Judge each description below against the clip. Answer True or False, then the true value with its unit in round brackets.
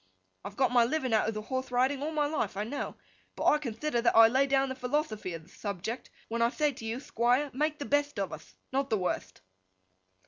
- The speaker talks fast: True (235 wpm)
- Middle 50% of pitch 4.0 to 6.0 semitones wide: True (4.3 semitones)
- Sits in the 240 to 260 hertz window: True (250 Hz)